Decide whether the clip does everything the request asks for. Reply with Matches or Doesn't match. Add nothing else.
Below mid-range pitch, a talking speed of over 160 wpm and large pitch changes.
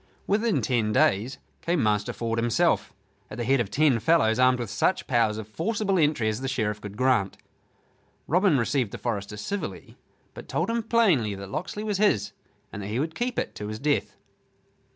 Matches